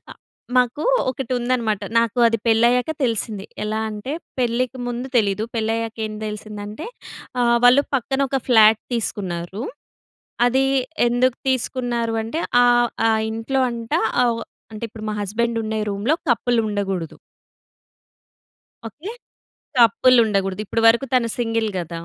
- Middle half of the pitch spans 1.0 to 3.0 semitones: Yes, narrow, 2.4 semitones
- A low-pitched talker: No, high, 230 Hz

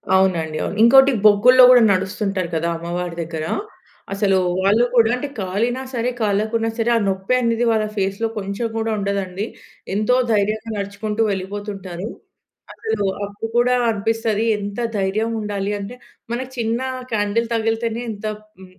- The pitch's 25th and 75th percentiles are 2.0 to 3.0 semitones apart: Yes, average, 2.7 semitones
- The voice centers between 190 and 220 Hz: Yes, high, 210 Hz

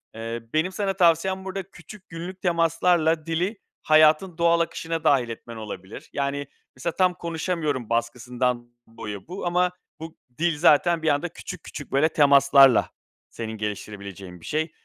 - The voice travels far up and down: Yes, wide, 6.0 semitones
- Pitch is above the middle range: No, medium, 155 Hz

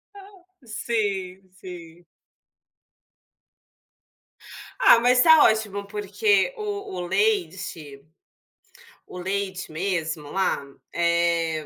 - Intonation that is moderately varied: No, wide, 6.1 semitones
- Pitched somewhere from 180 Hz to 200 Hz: Yes, high, 190 Hz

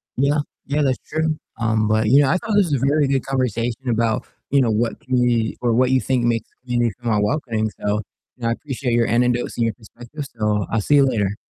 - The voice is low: Yes, low, 120 Hz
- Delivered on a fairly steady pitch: No, average, 3.1 semitones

